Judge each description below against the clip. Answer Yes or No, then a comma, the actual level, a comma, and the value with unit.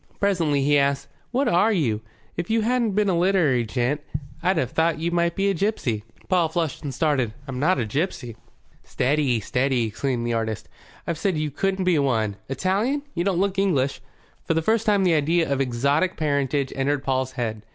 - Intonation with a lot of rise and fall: Yes, wide, 6.0 semitones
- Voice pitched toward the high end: No, medium, 150 Hz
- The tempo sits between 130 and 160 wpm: No, average, 195 wpm